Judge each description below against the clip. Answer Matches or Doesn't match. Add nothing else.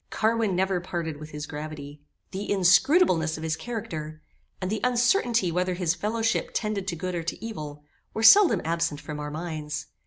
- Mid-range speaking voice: Matches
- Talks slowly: Doesn't match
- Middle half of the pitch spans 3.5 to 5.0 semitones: Doesn't match